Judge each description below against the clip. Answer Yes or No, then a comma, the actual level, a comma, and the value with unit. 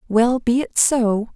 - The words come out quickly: No, average, 175 wpm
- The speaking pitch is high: Yes, high, 235 Hz